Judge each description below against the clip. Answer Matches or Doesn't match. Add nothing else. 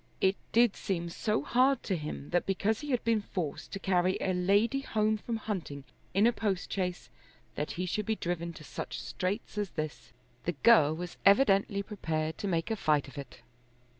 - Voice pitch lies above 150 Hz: Matches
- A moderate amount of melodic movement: Matches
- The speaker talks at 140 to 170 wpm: Doesn't match